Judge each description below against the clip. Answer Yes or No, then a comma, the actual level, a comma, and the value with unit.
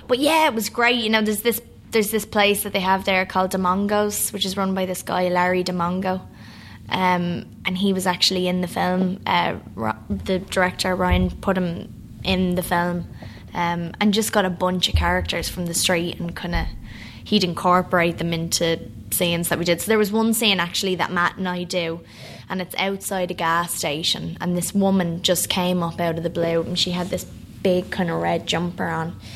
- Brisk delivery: Yes, fast, 210 wpm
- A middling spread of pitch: No, narrow, 2.1 semitones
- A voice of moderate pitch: Yes, medium, 180 Hz